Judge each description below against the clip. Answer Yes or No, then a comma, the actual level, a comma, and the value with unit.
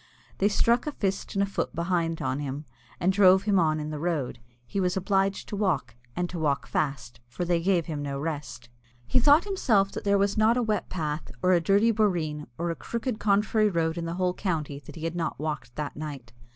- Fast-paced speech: Yes, fast, 225 wpm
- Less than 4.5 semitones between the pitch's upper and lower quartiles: No, average, 4.8 semitones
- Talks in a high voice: No, medium, 175 Hz